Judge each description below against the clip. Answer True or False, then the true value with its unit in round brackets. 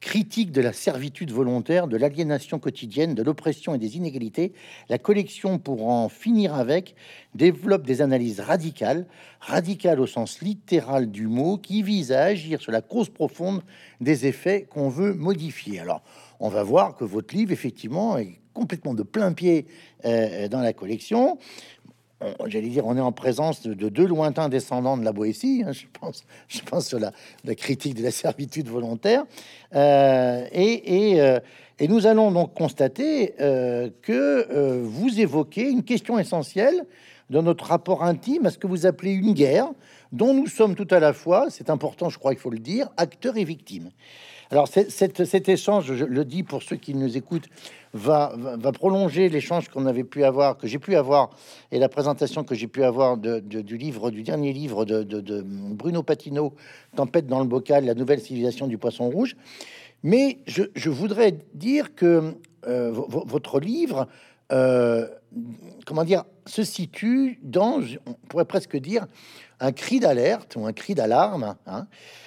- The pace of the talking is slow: False (175 wpm)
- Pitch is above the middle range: False (155 Hz)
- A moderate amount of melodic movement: False (7.0 semitones)